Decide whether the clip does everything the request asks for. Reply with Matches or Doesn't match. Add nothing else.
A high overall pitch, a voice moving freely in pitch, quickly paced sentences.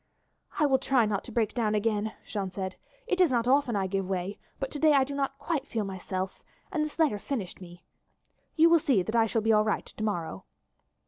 Matches